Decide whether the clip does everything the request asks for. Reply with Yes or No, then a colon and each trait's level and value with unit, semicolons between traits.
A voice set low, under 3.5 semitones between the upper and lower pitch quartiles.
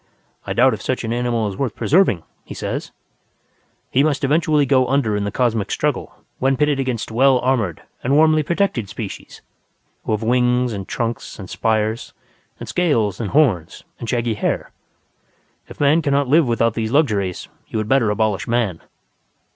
No: low, 120 Hz; average, 4.2 semitones